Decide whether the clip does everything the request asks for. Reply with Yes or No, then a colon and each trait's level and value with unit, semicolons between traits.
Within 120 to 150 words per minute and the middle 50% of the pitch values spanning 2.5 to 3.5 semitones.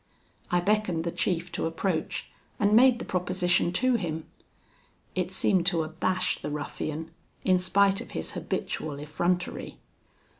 Yes: average, 140 wpm; average, 2.8 semitones